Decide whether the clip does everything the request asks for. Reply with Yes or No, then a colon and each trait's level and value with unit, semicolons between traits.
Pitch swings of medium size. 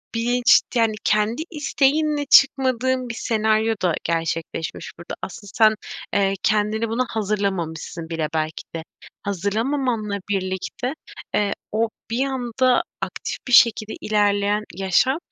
Yes: average, 4.0 semitones